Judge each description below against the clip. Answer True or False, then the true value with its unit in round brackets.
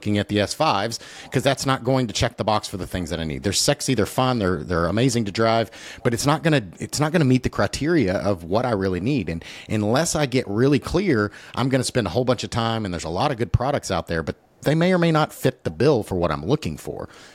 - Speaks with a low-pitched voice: True (115 Hz)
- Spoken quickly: True (285 wpm)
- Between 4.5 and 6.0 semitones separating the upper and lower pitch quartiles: True (5.4 semitones)